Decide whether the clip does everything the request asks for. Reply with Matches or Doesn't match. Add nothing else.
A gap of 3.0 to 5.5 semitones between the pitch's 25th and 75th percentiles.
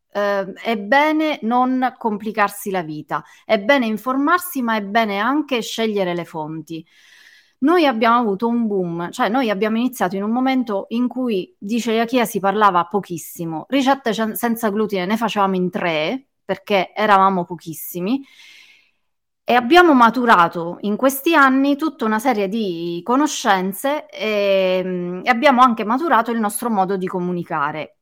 Matches